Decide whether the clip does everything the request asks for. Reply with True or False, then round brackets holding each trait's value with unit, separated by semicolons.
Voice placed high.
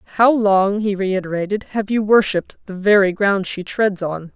True (195 Hz)